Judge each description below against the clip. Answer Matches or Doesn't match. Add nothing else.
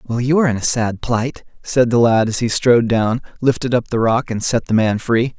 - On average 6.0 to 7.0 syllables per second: Doesn't match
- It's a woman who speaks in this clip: Doesn't match